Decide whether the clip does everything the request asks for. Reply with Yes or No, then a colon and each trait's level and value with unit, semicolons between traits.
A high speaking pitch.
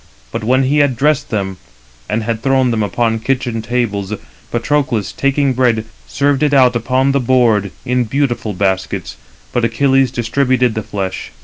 No: low, 125 Hz